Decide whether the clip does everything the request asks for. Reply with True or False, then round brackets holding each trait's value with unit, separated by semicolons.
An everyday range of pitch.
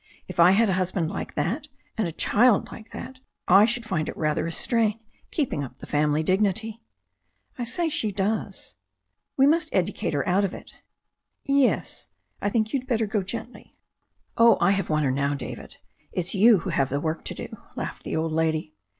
False (6.3 semitones)